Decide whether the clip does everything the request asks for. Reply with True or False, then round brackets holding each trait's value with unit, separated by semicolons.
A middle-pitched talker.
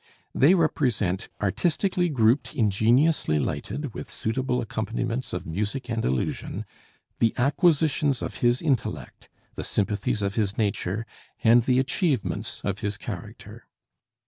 False (120 Hz)